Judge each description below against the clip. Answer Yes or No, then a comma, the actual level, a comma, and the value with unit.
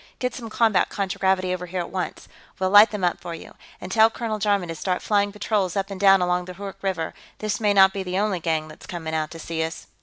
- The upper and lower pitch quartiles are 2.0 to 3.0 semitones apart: Yes, narrow, 2.5 semitones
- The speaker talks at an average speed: No, fast, 250 wpm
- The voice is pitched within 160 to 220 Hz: Yes, high, 190 Hz